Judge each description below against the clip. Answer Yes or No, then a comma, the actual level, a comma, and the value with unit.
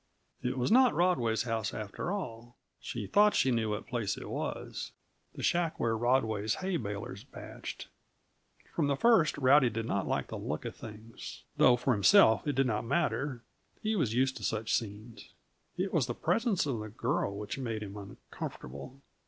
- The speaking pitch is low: Yes, low, 120 Hz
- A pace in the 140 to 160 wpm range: No, average, 175 wpm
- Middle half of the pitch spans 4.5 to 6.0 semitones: Yes, average, 4.8 semitones